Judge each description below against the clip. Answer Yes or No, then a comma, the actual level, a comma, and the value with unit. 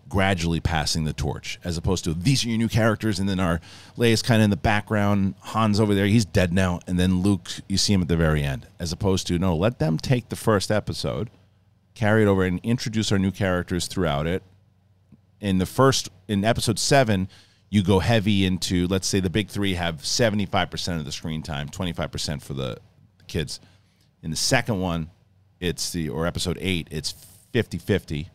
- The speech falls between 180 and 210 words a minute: Yes, average, 200 wpm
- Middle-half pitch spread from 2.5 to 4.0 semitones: Yes, average, 3.6 semitones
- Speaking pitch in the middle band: No, very low, 95 Hz